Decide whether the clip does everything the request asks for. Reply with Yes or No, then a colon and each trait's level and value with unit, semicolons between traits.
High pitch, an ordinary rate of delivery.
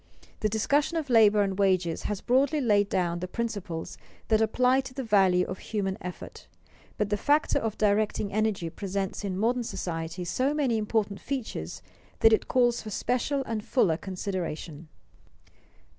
Yes: high, 210 Hz; average, 160 wpm